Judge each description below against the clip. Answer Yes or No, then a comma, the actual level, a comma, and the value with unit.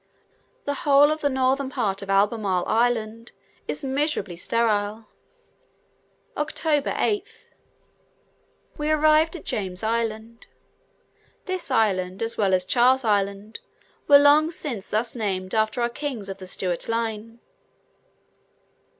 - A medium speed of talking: No, slow, 120 wpm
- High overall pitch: Yes, high, 230 Hz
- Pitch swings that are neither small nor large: No, wide, 5.7 semitones